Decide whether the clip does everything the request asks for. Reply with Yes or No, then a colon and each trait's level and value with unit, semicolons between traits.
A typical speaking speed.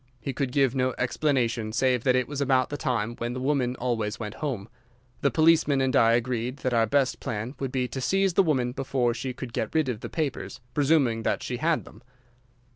No: fast, 215 wpm